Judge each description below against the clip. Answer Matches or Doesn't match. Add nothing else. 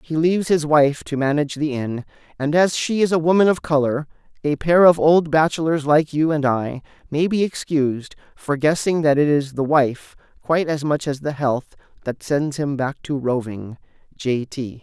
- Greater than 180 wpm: Matches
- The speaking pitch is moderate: Matches